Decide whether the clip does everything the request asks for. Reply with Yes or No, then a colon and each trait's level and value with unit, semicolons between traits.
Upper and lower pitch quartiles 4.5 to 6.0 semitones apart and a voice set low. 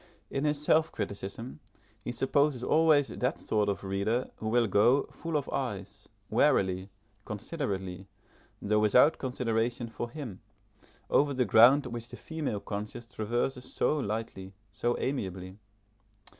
Yes: average, 5.0 semitones; low, 120 Hz